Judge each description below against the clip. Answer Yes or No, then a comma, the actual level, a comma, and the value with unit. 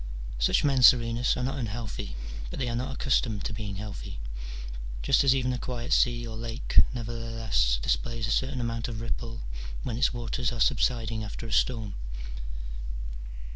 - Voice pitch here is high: No, low, 115 Hz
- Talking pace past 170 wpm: No, average, 165 wpm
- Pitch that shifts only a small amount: Yes, narrow, 1.9 semitones